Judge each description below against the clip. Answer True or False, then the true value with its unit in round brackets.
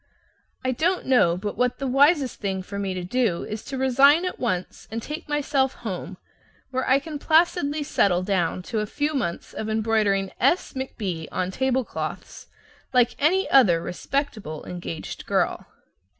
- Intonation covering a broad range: True (6.4 semitones)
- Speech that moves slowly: False (165 wpm)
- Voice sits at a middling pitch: False (245 Hz)